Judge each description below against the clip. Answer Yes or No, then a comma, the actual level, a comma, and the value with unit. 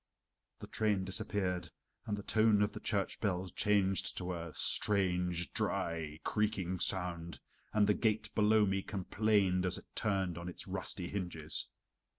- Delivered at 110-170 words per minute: Yes, average, 150 wpm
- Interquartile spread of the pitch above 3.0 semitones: No, average, 2.7 semitones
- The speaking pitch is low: Yes, very low, 95 Hz